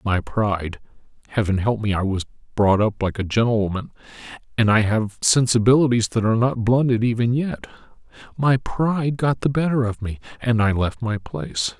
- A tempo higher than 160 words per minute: Yes, average, 170 wpm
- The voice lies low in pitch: Yes, low, 115 Hz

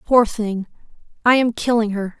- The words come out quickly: No, average, 165 wpm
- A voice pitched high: Yes, high, 220 Hz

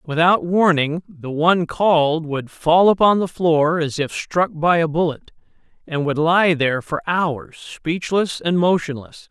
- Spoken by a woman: No, male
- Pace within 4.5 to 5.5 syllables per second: No, 4.2 syllables/s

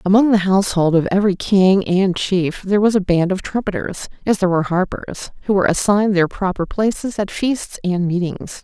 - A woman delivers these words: Yes, female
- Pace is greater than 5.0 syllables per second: Yes, 5.5 syllables/s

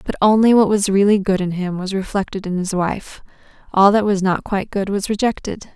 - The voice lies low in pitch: No, high, 195 Hz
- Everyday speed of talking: No, fast, 220 wpm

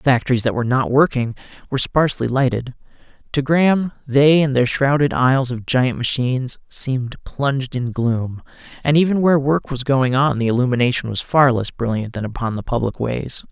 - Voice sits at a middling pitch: No, low, 130 Hz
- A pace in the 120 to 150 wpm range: No, average, 180 wpm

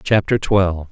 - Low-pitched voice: Yes, very low, 95 Hz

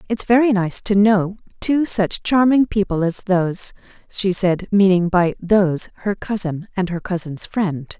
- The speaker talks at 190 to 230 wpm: No, average, 165 wpm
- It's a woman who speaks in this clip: Yes, female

